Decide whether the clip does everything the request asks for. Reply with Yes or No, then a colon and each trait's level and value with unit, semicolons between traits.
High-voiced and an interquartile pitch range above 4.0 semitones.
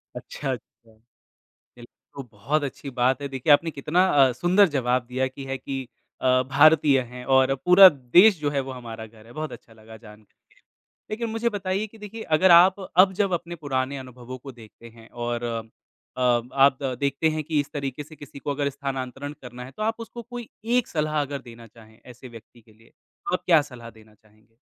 No: low, 135 Hz; average, 4.8 semitones